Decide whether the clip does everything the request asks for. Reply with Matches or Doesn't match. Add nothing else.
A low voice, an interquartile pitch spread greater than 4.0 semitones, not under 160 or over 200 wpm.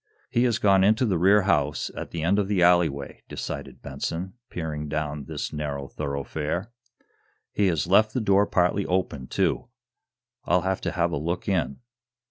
Matches